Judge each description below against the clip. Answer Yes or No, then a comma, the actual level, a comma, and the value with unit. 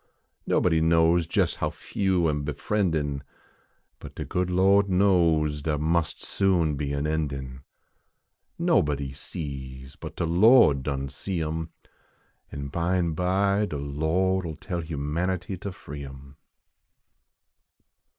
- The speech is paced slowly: Yes, slow, 130 wpm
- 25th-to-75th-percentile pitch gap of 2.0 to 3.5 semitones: No, average, 4.1 semitones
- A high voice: No, very low, 80 Hz